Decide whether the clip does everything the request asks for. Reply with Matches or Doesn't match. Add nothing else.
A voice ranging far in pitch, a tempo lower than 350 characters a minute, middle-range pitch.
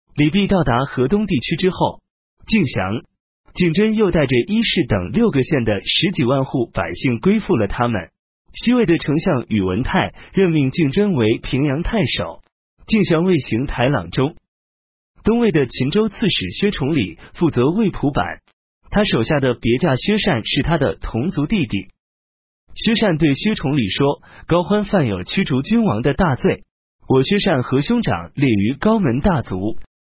Matches